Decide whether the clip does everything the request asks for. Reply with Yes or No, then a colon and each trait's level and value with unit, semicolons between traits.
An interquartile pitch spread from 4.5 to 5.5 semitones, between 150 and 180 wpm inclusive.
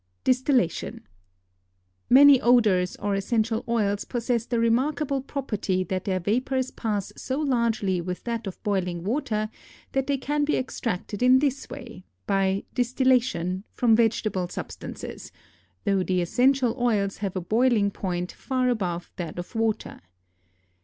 No: average, 5.0 semitones; slow, 135 wpm